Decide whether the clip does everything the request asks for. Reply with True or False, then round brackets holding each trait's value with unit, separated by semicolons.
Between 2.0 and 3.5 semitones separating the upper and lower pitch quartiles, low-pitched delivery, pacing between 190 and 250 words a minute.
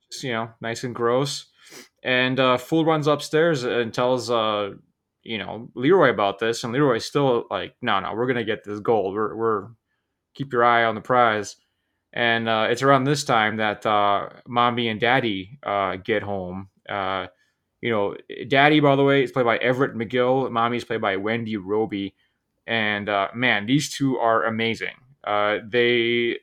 False (3.2 semitones; 115 Hz; 175 wpm)